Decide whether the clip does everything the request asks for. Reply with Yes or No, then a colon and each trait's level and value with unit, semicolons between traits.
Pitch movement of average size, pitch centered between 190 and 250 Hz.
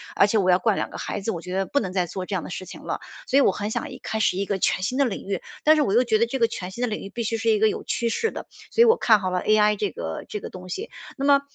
Yes: average, 4.0 semitones; high, 210 Hz